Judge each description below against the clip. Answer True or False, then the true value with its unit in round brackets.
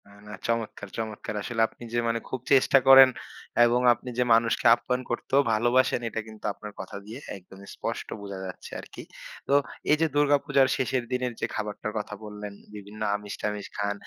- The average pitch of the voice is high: False (115 Hz)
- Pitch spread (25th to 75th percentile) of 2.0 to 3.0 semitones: False (3.4 semitones)